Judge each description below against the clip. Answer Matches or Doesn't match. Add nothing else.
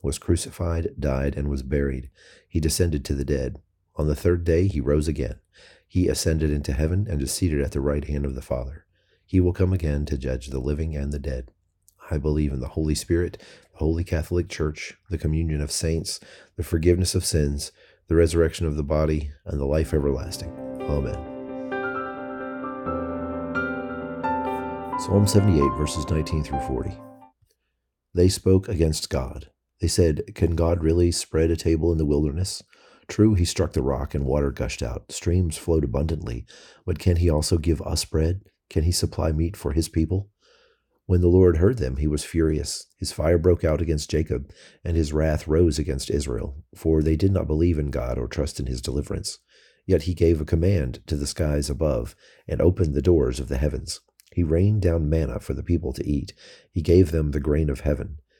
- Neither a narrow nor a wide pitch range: Matches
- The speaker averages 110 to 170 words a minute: Doesn't match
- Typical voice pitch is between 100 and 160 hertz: Doesn't match